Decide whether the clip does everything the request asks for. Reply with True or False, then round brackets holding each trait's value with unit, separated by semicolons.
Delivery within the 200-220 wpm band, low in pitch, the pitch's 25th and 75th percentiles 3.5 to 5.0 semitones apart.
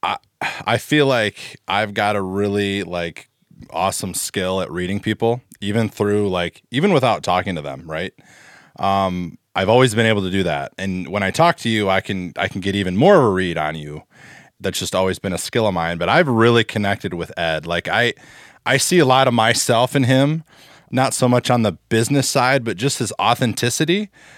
True (205 wpm; 110 Hz; 4.7 semitones)